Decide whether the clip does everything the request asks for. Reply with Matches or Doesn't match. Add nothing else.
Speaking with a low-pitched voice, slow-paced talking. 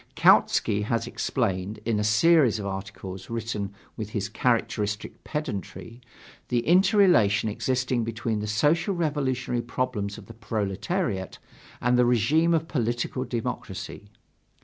Matches